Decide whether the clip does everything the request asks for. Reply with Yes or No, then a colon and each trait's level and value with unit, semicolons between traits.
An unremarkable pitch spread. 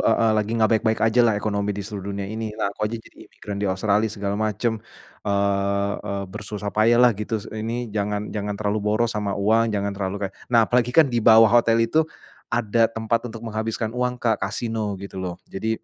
No: narrow, 2.0 semitones